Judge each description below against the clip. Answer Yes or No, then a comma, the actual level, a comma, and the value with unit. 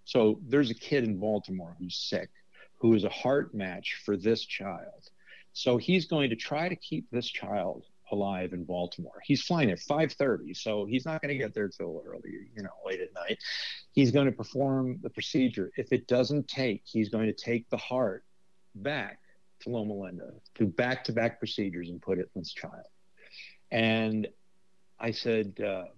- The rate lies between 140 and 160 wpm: No, average, 185 wpm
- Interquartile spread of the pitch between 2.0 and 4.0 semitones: No, average, 4.9 semitones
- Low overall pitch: Yes, low, 115 Hz